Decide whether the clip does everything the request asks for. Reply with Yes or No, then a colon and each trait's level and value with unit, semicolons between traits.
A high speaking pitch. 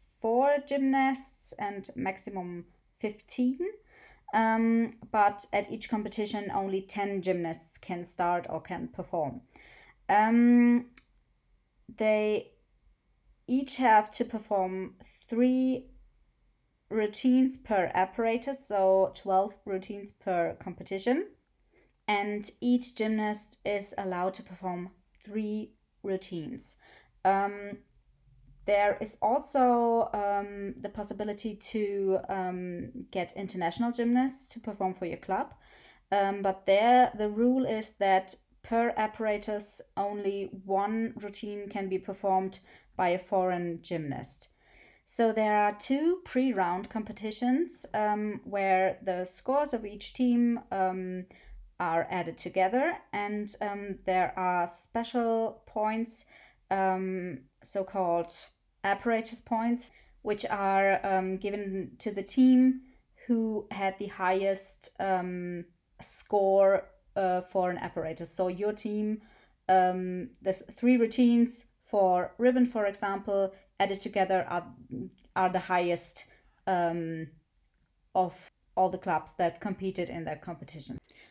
Yes: high, 205 Hz